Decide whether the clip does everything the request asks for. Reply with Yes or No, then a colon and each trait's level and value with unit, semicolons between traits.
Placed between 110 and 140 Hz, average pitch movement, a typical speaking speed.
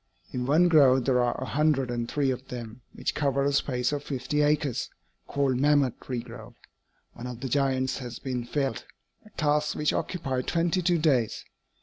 Yes: low, 135 Hz; average, 3.0 semitones; average, 185 wpm